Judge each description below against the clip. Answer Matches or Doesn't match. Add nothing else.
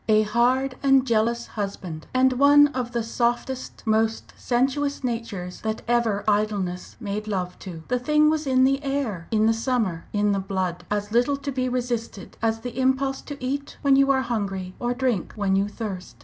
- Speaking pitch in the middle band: Doesn't match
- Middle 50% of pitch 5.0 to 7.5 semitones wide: Doesn't match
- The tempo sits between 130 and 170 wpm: Doesn't match